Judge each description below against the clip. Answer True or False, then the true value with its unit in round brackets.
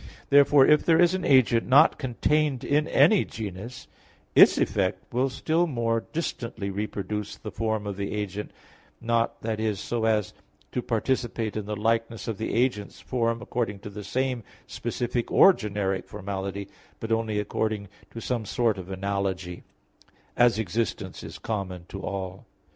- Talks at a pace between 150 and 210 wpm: True (155 wpm)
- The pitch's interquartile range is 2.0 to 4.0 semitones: True (3.4 semitones)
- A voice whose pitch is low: True (110 Hz)